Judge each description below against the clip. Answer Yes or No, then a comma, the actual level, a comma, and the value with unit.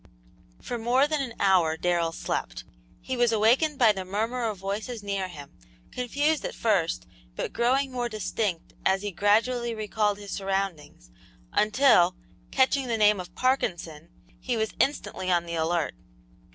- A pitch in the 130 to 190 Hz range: No, high, 210 Hz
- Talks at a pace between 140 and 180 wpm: Yes, average, 150 wpm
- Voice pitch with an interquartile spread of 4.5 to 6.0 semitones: Yes, average, 5.1 semitones